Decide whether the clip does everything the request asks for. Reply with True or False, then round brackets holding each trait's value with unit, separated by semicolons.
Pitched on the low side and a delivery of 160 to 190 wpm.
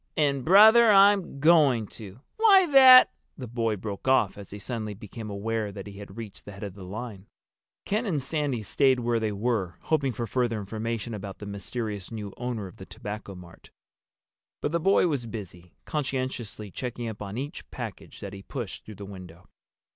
True (115 Hz; 185 wpm)